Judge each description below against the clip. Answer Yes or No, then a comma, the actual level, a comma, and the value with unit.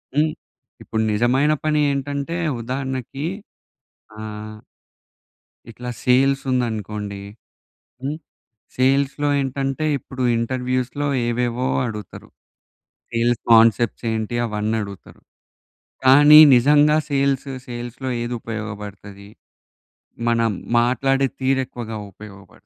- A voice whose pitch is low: Yes, low, 125 Hz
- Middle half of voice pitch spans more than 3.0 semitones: Yes, average, 3.6 semitones